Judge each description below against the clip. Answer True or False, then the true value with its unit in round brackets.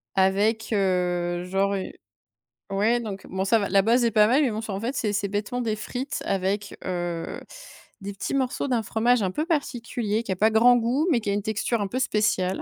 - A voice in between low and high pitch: False (210 Hz)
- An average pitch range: True (3.4 semitones)